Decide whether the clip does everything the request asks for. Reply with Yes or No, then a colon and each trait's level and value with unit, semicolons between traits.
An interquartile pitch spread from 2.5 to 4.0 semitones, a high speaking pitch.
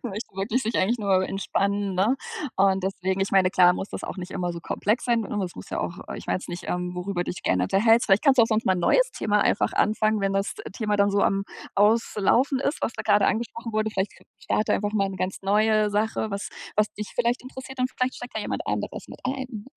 Yes: average, 2.8 semitones; high, 205 Hz